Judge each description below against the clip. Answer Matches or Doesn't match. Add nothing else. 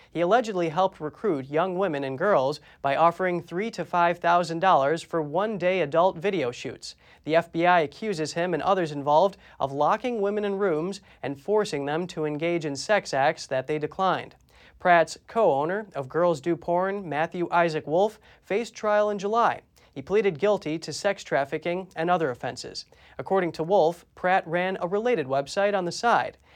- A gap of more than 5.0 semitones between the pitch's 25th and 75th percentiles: Doesn't match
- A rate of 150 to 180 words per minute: Matches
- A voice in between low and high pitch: Matches